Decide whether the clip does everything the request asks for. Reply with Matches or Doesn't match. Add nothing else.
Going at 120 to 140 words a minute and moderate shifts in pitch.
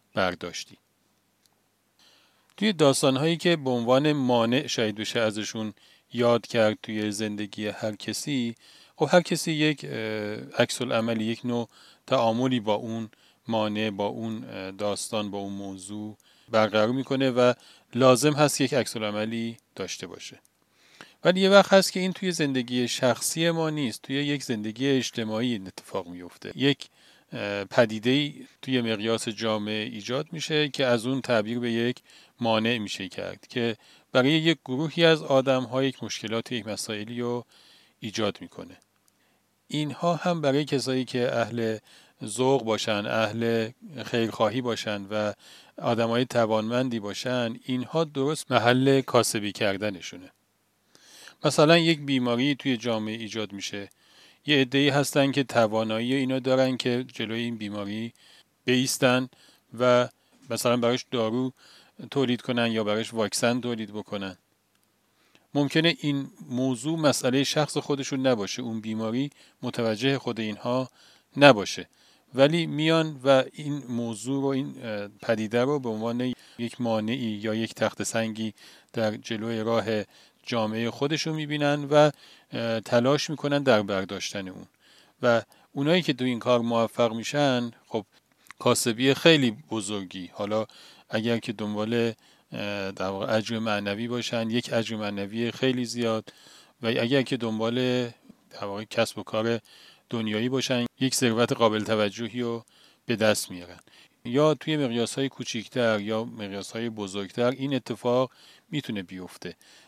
Matches